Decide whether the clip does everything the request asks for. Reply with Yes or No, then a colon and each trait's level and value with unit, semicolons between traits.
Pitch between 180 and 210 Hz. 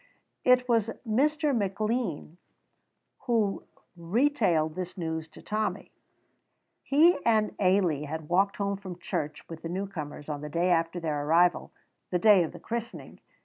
Yes: medium, 185 Hz